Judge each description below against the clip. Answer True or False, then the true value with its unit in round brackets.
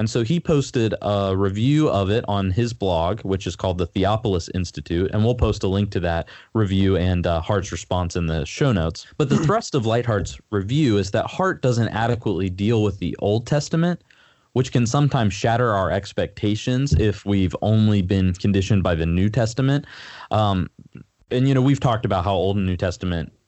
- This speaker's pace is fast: False (195 wpm)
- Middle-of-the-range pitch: False (100 Hz)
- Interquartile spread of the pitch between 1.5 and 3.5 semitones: False (4.1 semitones)